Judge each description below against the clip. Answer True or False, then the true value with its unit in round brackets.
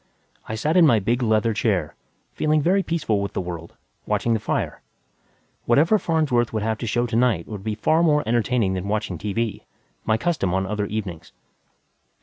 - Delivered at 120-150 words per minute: False (180 wpm)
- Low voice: True (110 Hz)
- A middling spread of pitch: True (3.9 semitones)